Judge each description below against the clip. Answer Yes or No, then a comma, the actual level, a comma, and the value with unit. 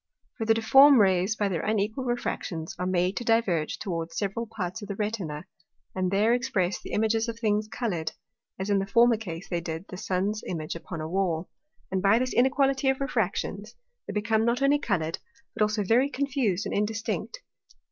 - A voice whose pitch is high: Yes, high, 210 Hz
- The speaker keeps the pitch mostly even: No, average, 4.1 semitones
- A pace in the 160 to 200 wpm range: Yes, average, 190 wpm